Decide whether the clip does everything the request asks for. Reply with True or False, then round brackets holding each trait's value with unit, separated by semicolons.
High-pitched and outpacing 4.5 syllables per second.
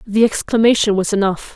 True (210 Hz; 5.6 syllables/s)